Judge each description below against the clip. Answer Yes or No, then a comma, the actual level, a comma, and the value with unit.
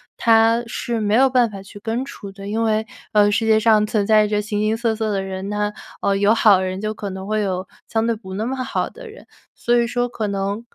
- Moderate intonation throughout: No, narrow, 2.1 semitones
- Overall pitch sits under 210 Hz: No, high, 215 Hz